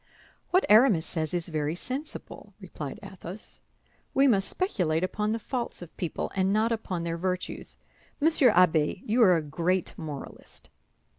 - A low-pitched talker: No, medium, 185 Hz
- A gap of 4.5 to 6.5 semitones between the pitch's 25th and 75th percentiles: Yes, average, 5.2 semitones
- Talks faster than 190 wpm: No, average, 150 wpm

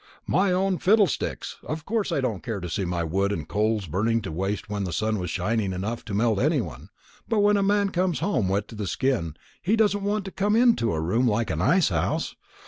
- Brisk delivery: Yes, fast, 230 wpm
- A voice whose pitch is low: Yes, low, 115 Hz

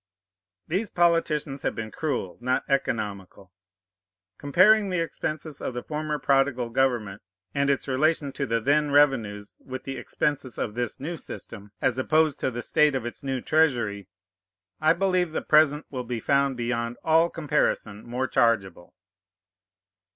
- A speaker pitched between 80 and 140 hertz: Yes, low, 135 Hz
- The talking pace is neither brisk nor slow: Yes, average, 150 wpm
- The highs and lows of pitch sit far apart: No, average, 4.5 semitones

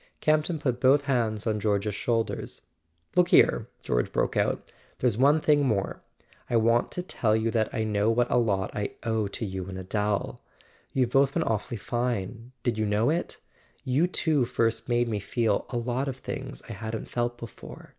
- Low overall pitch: Yes, low, 115 Hz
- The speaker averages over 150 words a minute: Yes, average, 185 wpm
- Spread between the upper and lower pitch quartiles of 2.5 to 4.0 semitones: Yes, average, 3.2 semitones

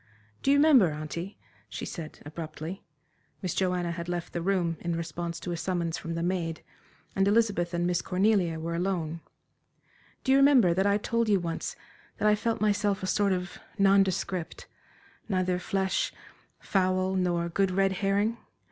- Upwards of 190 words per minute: No, average, 165 wpm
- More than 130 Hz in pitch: Yes, medium, 185 Hz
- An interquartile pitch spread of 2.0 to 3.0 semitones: Yes, average, 2.7 semitones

